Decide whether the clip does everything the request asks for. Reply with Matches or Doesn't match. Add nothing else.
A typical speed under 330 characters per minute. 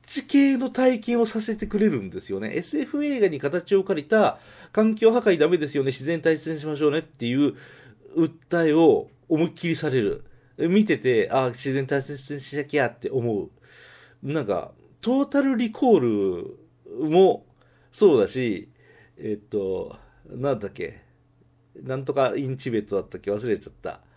Matches